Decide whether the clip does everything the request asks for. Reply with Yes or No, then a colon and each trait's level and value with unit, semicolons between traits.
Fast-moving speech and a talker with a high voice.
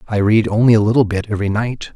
No: fast, 245 wpm; low, 110 Hz